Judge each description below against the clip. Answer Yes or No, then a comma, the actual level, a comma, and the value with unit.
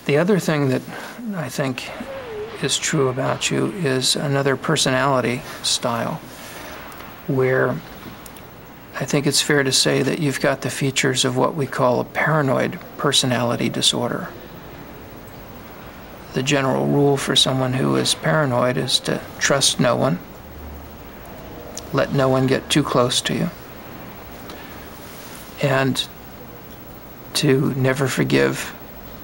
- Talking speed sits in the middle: No, slow, 120 wpm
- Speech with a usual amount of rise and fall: No, narrow, 2.0 semitones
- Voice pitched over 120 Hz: Yes, low, 135 Hz